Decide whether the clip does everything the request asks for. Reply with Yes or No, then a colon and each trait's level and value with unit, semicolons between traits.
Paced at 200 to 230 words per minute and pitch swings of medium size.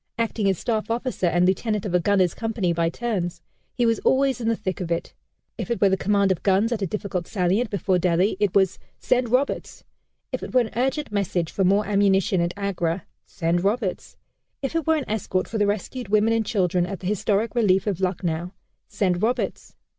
Yes: fast, 205 wpm; average, 3.7 semitones